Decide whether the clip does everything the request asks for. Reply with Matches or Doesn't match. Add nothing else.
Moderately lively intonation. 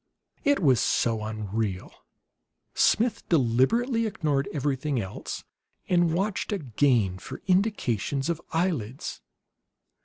Doesn't match